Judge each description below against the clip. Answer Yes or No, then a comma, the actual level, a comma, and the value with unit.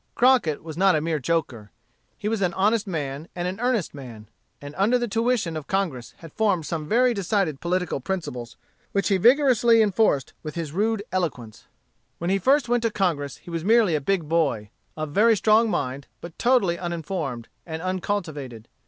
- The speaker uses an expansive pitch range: Yes, wide, 6.1 semitones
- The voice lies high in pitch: No, medium, 175 Hz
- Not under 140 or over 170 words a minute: No, average, 180 wpm